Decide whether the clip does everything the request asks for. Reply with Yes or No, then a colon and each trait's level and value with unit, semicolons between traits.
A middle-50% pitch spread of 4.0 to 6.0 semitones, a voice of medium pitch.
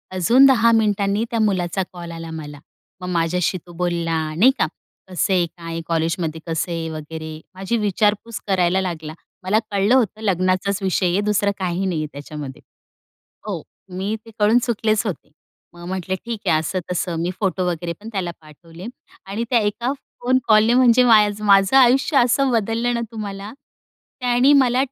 No: average, 4.6 semitones; high, 195 Hz